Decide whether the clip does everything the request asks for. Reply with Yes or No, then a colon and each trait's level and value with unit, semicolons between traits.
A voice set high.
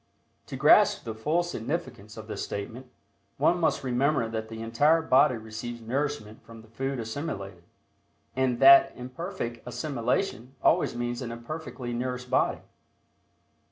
No: low, 125 Hz